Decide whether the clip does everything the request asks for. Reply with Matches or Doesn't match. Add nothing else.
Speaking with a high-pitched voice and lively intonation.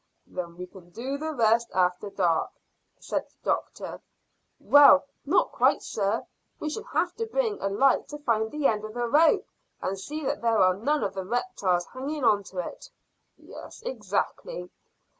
Matches